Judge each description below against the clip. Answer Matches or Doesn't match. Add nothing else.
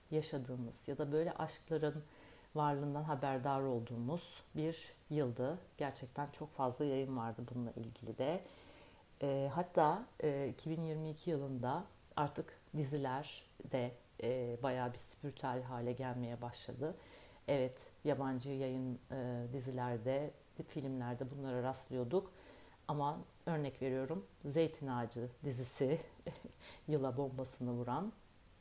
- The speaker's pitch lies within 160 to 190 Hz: Doesn't match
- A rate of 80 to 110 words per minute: Matches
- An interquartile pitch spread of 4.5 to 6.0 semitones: Doesn't match